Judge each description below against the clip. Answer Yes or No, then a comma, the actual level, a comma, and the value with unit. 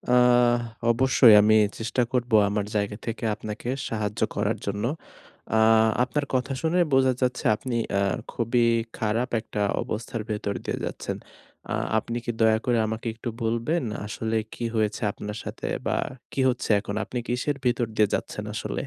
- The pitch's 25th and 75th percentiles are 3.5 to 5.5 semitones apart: No, narrow, 2.6 semitones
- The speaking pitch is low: Yes, low, 115 Hz